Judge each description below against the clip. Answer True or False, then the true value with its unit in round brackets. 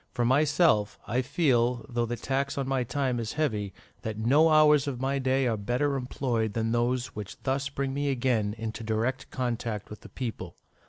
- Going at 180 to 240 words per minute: True (190 wpm)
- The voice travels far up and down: False (3.3 semitones)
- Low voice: True (125 Hz)